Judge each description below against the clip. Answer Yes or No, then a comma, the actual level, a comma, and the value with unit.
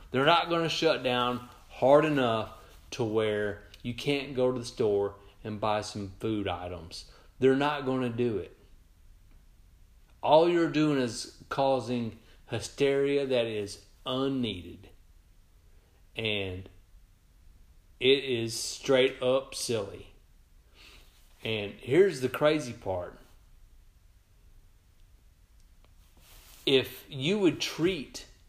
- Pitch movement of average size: No, wide, 6.5 semitones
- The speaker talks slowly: Yes, slow, 105 wpm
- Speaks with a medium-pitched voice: No, low, 105 Hz